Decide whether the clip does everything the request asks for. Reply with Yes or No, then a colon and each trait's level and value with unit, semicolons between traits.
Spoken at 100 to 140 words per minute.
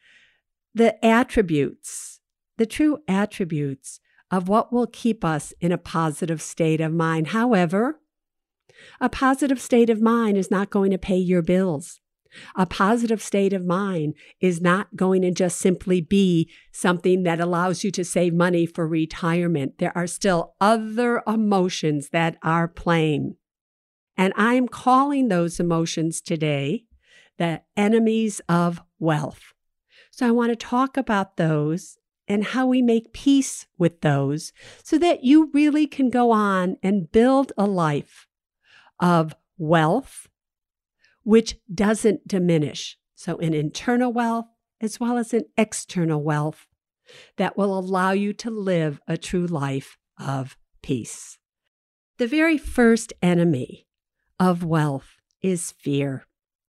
Yes: slow, 135 wpm